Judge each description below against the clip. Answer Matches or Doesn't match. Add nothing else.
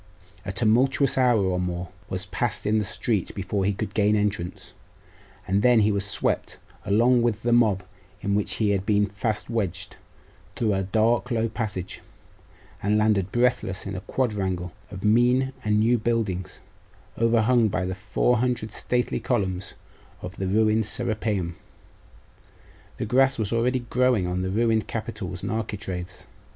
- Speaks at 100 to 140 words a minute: Doesn't match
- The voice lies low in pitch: Matches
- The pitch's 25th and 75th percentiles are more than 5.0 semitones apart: Doesn't match